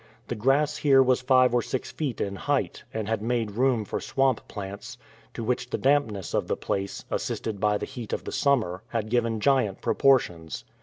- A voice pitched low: Yes, low, 120 Hz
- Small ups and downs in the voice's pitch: No, average, 4.1 semitones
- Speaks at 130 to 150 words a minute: No, average, 190 wpm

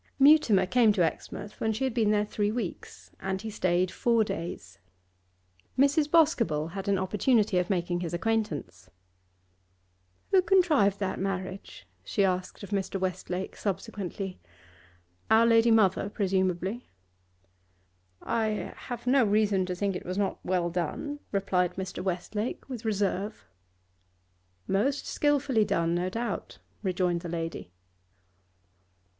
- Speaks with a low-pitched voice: No, high, 200 Hz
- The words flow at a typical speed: No, slow, 130 wpm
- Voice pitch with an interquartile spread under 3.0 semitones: No, average, 3.8 semitones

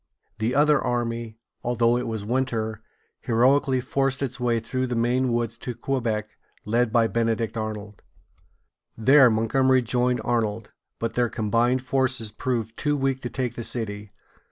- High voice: No, low, 120 Hz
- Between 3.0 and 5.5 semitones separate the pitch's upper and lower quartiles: No, narrow, 2.4 semitones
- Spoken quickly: No, average, 150 wpm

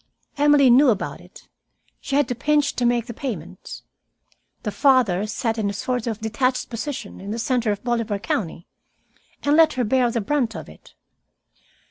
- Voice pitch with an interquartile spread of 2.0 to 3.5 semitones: No, average, 3.9 semitones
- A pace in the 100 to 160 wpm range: No, average, 175 wpm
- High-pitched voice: Yes, high, 240 Hz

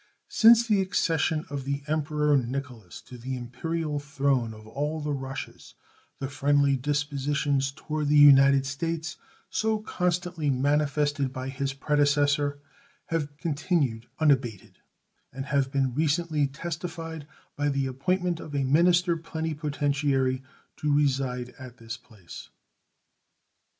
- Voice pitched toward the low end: No, medium, 145 Hz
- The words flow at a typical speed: No, slow, 120 wpm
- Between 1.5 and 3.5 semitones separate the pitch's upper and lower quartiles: Yes, narrow, 2.6 semitones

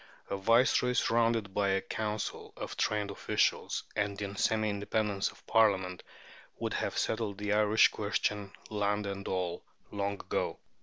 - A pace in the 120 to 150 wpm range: Yes, average, 145 wpm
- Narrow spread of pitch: Yes, narrow, 1.7 semitones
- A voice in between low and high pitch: No, low, 105 Hz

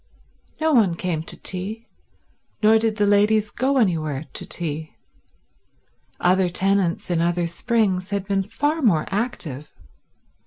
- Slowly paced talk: Yes, slow, 130 wpm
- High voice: Yes, high, 195 Hz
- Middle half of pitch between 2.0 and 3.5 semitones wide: No, average, 4.3 semitones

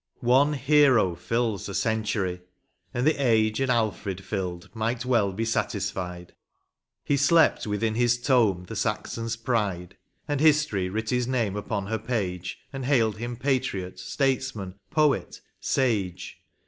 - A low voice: Yes, low, 115 Hz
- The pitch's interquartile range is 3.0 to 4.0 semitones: No, average, 4.6 semitones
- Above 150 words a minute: No, average, 140 wpm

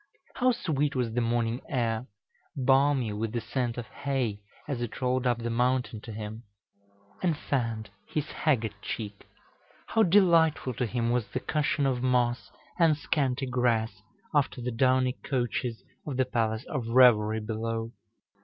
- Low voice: Yes, low, 125 Hz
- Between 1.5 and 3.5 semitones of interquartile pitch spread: Yes, average, 2.9 semitones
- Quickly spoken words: No, average, 155 wpm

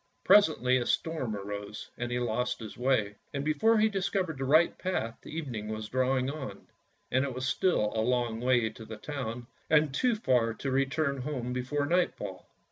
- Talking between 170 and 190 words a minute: Yes, average, 180 wpm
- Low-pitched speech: Yes, low, 130 Hz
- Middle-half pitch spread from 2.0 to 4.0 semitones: No, average, 4.8 semitones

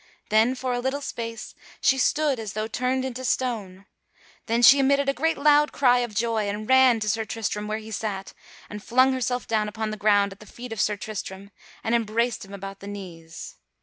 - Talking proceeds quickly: Yes, fast, 210 wpm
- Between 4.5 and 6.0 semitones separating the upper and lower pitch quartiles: No, average, 3.6 semitones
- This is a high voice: Yes, high, 225 Hz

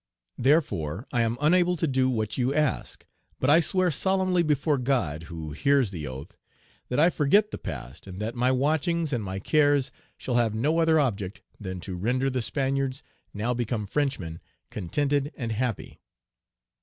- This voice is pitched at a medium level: No, low, 130 Hz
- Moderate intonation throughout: No, wide, 6.2 semitones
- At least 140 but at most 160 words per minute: No, average, 170 wpm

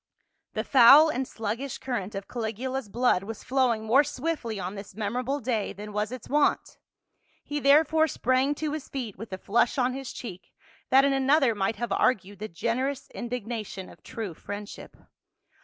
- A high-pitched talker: Yes, high, 240 Hz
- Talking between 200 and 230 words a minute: No, average, 170 wpm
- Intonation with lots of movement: No, average, 4.3 semitones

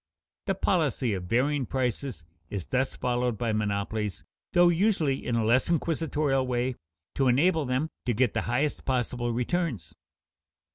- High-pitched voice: No, low, 125 Hz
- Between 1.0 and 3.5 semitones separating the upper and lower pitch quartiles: No, average, 4.2 semitones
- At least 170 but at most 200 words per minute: No, average, 145 wpm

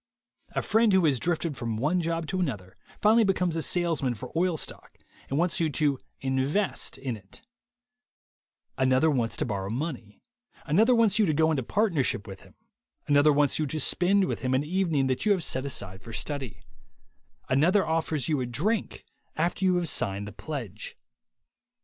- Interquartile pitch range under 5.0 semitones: No, wide, 5.4 semitones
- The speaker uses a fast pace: No, average, 180 wpm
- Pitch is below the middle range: No, medium, 150 Hz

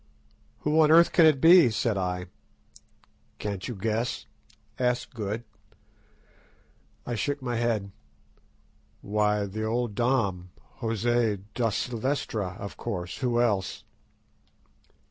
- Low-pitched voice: Yes, low, 115 Hz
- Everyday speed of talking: No, slow, 105 wpm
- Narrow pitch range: No, average, 3.4 semitones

